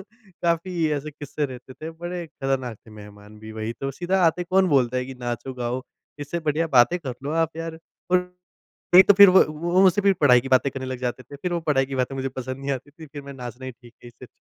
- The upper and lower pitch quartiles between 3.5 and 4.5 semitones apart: No, average, 4.9 semitones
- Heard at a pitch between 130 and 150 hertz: Yes, medium, 140 Hz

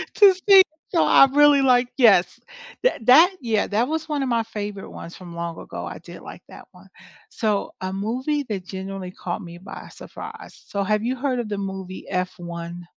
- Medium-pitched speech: No, high, 210 Hz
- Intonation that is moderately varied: No, wide, 5.7 semitones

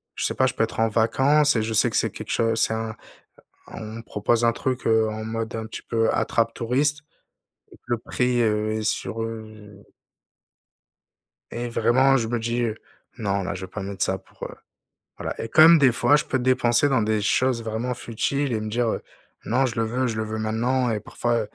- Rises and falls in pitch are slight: Yes, narrow, 2.3 semitones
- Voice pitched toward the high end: No, low, 115 Hz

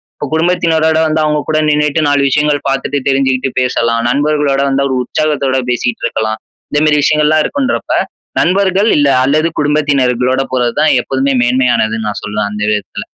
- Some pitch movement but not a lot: Yes, average, 3.3 semitones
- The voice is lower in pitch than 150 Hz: Yes, medium, 140 Hz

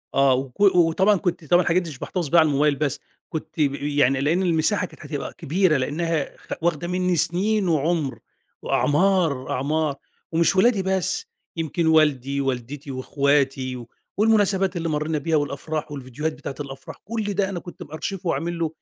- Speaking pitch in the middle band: Yes, medium, 155 Hz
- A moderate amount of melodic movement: Yes, average, 4.0 semitones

